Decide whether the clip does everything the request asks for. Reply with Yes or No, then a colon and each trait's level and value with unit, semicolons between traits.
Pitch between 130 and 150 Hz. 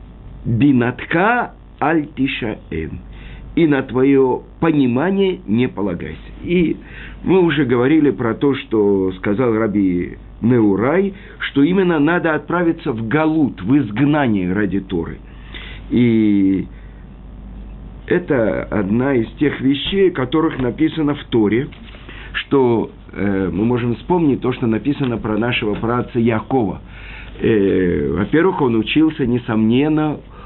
No: low, 120 Hz